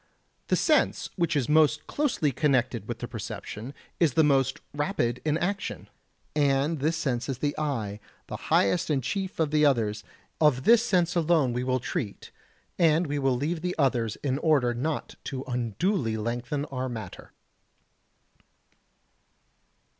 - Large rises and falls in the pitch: No, average, 4.5 semitones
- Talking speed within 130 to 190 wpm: Yes, average, 150 wpm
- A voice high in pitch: No, medium, 140 Hz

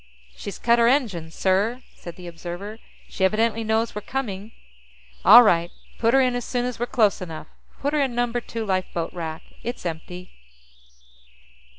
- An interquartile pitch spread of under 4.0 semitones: No, average, 5.1 semitones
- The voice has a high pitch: Yes, high, 215 Hz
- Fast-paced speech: No, average, 170 wpm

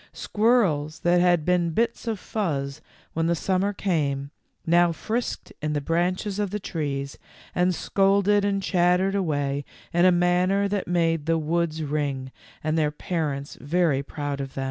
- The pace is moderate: Yes, average, 160 wpm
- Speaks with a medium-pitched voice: Yes, medium, 170 Hz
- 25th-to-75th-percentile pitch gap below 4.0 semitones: No, average, 4.3 semitones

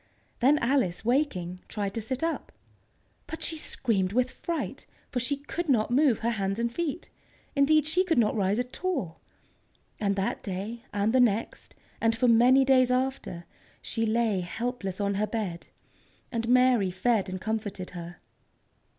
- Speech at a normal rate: Yes, average, 160 wpm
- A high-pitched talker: Yes, high, 230 Hz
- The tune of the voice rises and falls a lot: No, average, 4.6 semitones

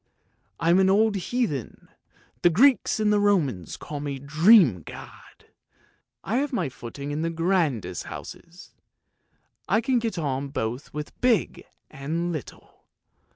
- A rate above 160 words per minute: No, average, 140 wpm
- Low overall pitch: No, medium, 165 Hz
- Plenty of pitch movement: Yes, wide, 6.8 semitones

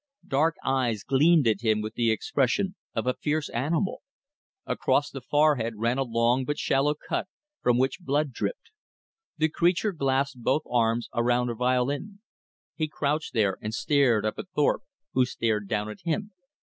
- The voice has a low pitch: Yes, low, 130 Hz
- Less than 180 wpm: Yes, average, 165 wpm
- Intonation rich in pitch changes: No, average, 4.5 semitones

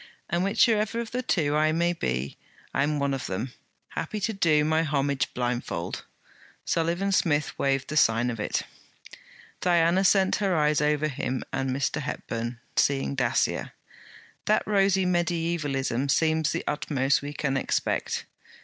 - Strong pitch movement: No, average, 4.4 semitones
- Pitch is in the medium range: Yes, medium, 150 Hz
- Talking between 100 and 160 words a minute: Yes, average, 145 wpm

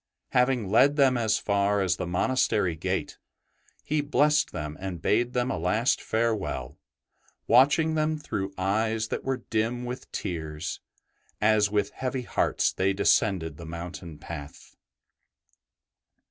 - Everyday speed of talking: No, slow, 130 wpm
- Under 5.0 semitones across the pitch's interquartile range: No, wide, 5.5 semitones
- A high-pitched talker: No, low, 110 Hz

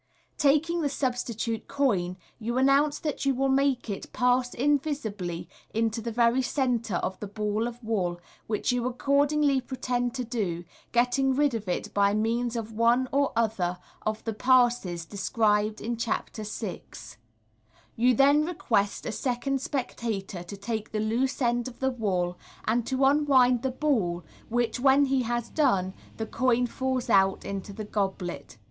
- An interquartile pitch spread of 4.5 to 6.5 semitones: No, average, 3.9 semitones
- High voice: Yes, high, 235 Hz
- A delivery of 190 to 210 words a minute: No, average, 160 wpm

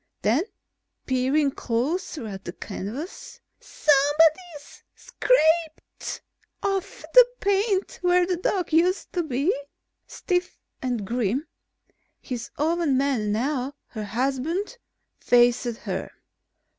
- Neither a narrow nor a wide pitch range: No, wide, 6.4 semitones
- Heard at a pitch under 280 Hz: No, very high, 290 Hz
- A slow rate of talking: Yes, slow, 100 wpm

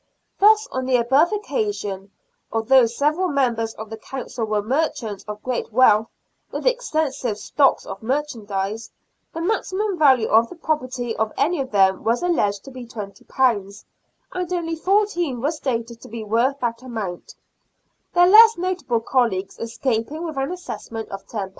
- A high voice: Yes, very high, 255 Hz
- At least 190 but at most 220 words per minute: No, average, 160 wpm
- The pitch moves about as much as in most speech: No, wide, 6.5 semitones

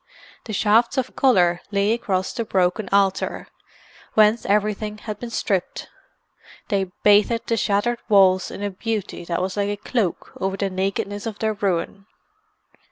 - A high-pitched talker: Yes, high, 205 Hz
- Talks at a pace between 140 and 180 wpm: Yes, average, 155 wpm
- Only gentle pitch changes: Yes, narrow, 2.2 semitones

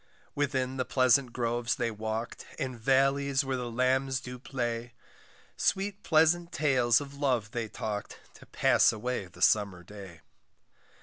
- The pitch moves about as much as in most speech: Yes, average, 3.0 semitones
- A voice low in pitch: Yes, low, 125 Hz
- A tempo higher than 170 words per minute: No, average, 140 wpm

